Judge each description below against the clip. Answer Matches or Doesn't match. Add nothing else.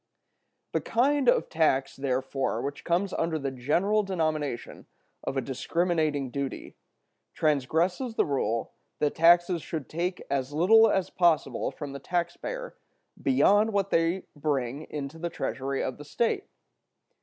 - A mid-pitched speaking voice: Matches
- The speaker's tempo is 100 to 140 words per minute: Matches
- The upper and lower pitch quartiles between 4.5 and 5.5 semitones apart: Matches